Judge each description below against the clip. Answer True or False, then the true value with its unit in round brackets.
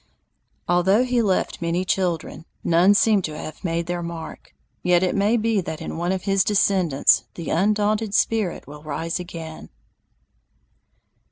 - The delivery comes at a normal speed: True (150 wpm)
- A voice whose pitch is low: False (180 Hz)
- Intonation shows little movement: False (3.5 semitones)